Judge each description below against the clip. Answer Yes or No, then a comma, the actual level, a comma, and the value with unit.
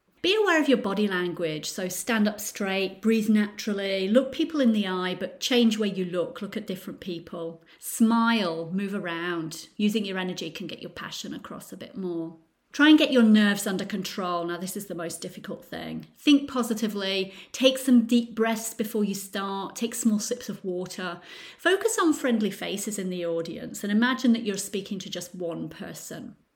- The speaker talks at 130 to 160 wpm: No, average, 190 wpm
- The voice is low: No, high, 200 Hz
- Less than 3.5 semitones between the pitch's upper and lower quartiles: No, average, 4.1 semitones